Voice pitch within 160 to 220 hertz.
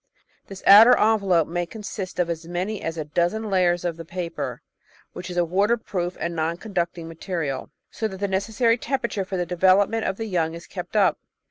Yes: medium, 185 Hz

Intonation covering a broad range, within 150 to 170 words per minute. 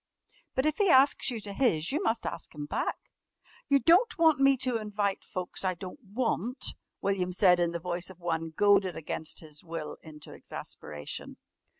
No: wide, 7.3 semitones; average, 180 wpm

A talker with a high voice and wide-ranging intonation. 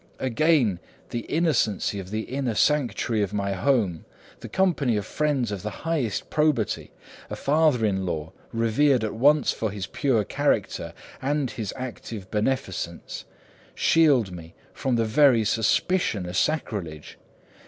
No: low, 115 Hz; wide, 5.8 semitones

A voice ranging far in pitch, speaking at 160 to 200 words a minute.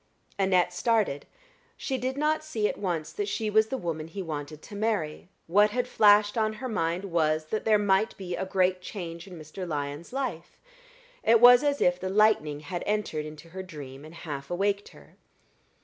No: average, 4.9 semitones; average, 190 wpm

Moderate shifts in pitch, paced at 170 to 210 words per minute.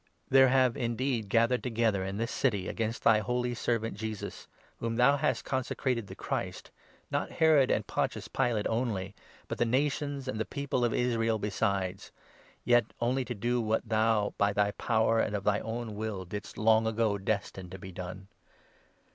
Yes: average, 3.0 semitones; average, 180 wpm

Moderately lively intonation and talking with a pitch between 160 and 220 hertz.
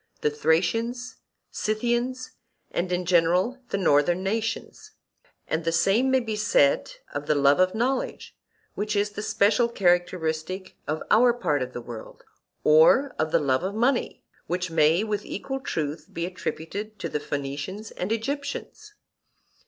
No: wide, 6.2 semitones; medium, 185 Hz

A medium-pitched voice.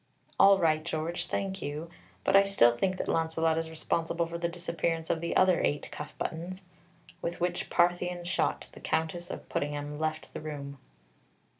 Yes: medium, 165 Hz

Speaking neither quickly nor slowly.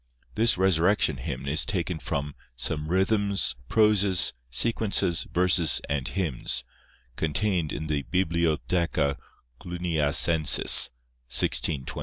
No: slow, 95 wpm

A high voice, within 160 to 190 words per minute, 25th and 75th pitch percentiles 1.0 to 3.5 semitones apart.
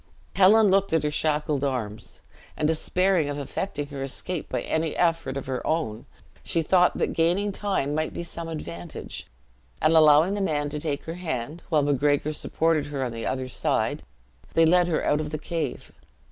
No: medium, 155 Hz; average, 185 wpm; average, 2.9 semitones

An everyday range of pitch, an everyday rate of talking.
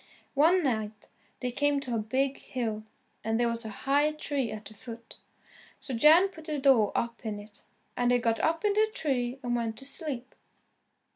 Yes: average, 4.3 semitones; average, 195 wpm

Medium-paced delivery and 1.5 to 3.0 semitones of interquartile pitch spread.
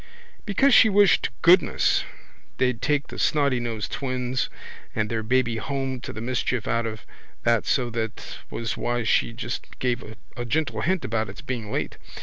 No: average, 165 wpm; average, 3.4 semitones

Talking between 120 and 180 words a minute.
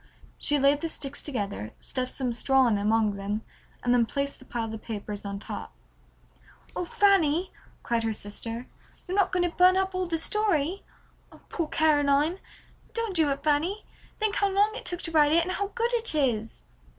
No: average, 190 wpm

